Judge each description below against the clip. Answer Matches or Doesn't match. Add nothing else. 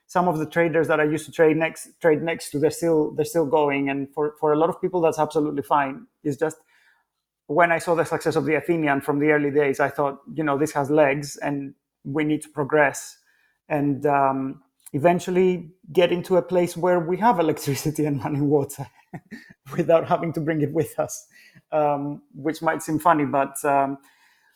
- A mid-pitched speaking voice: Matches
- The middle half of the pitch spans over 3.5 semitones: Doesn't match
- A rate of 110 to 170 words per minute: Doesn't match